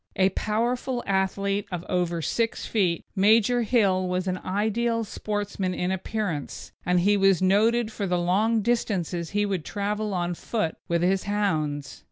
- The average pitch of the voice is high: Yes, high, 195 Hz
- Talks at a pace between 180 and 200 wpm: No, average, 155 wpm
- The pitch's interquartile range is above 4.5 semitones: No, average, 3.1 semitones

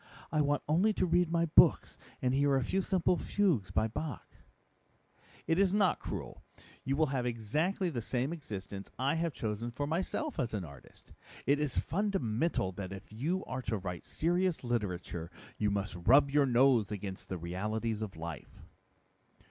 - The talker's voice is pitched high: No, low, 130 Hz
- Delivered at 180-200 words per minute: No, average, 170 wpm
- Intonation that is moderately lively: No, wide, 7.7 semitones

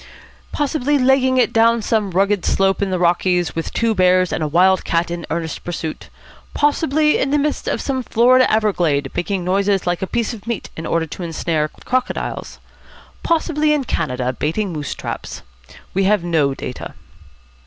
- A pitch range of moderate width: No, wide, 6.7 semitones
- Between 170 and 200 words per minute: Yes, average, 175 wpm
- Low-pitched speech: No, high, 195 Hz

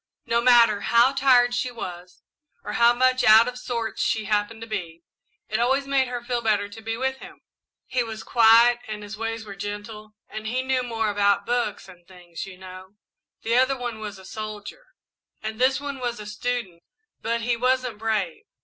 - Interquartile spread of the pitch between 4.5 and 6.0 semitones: No, average, 3.0 semitones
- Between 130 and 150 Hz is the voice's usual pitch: No, high, 225 Hz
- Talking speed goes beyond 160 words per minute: Yes, average, 200 wpm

